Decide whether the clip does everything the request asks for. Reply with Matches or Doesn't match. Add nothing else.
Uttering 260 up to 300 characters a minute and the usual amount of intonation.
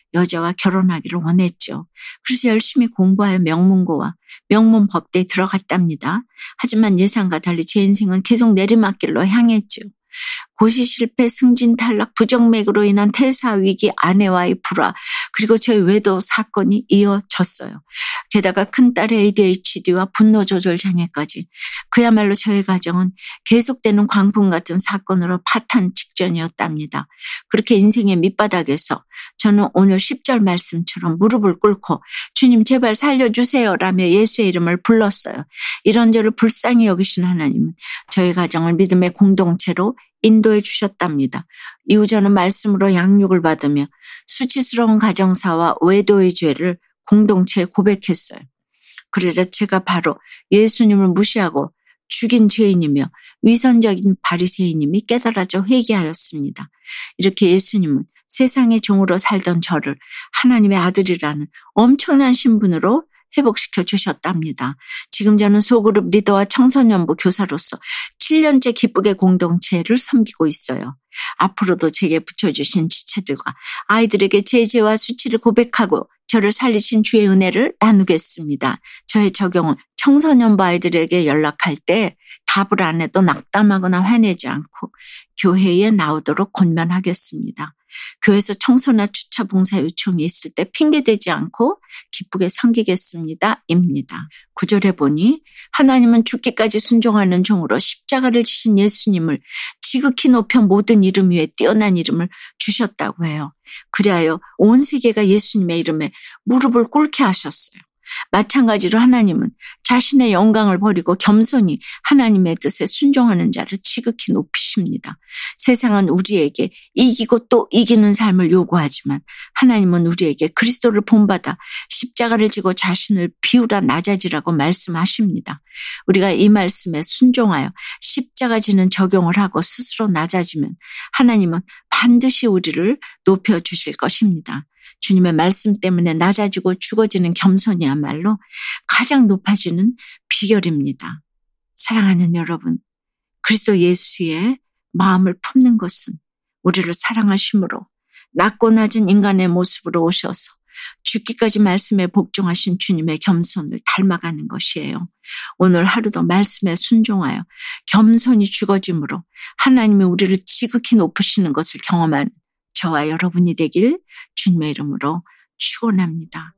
Doesn't match